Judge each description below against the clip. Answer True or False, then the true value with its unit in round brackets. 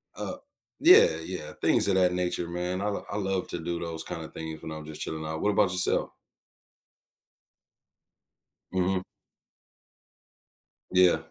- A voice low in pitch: True (90 Hz)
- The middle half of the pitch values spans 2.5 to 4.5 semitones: True (2.8 semitones)